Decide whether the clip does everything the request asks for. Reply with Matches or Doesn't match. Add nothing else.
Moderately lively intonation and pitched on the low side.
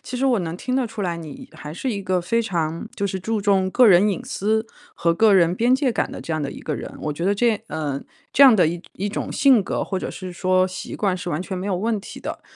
Doesn't match